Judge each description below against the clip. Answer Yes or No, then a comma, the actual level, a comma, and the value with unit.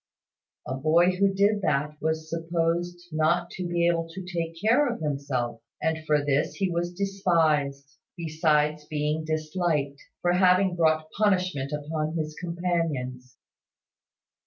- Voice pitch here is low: No, medium, 160 Hz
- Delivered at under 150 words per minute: Yes, slow, 135 wpm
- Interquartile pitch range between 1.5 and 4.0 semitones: Yes, average, 2.7 semitones